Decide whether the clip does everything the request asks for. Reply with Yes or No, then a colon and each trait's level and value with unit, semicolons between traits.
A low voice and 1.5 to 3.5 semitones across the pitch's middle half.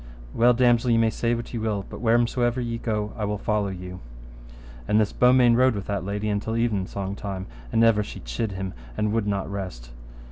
Yes: low, 105 Hz; average, 2.8 semitones